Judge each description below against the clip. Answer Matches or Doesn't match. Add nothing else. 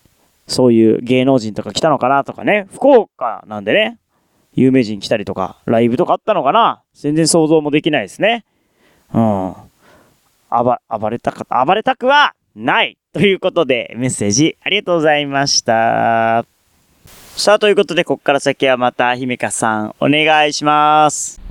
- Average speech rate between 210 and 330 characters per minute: Matches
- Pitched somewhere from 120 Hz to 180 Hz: Matches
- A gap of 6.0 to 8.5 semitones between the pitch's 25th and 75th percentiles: Matches